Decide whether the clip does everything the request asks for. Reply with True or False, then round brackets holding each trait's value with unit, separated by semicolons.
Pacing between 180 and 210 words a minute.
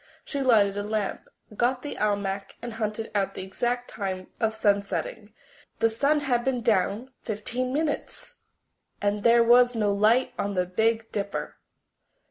False (150 wpm)